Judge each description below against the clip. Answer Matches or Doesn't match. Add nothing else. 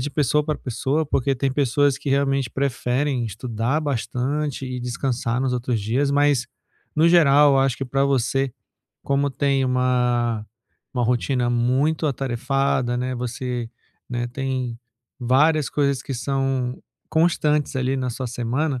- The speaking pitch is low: Matches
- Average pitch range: Doesn't match